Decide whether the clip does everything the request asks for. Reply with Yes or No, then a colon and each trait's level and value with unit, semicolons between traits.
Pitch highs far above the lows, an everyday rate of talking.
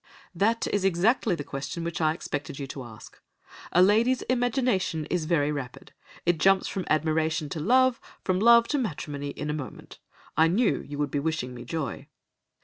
Yes: wide, 6.0 semitones; average, 180 wpm